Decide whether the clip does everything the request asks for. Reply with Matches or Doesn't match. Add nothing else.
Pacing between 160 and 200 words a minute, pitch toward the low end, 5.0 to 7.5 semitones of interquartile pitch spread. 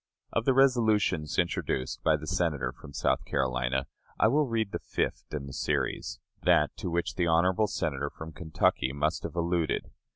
Matches